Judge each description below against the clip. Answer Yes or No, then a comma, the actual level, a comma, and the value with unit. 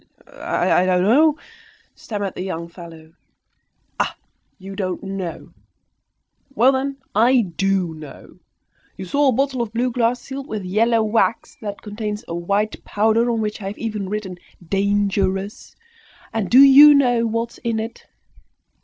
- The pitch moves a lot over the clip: No, average, 3.5 semitones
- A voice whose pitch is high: Yes, high, 210 Hz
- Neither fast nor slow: Yes, average, 150 wpm